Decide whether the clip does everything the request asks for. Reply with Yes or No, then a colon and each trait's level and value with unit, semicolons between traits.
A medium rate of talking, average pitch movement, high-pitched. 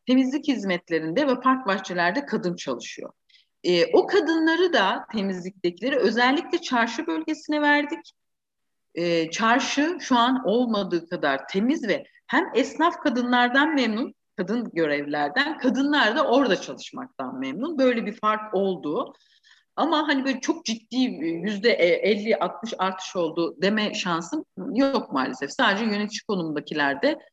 No: average, 120 wpm; wide, 7.5 semitones; high, 245 Hz